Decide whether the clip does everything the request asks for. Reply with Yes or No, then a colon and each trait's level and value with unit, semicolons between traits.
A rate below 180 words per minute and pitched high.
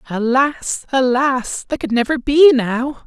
Yes: slow, 135 wpm; very high, 260 Hz